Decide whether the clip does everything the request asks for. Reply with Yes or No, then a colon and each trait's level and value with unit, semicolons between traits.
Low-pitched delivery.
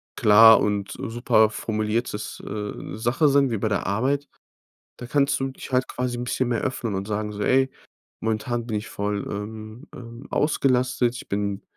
Yes: low, 115 Hz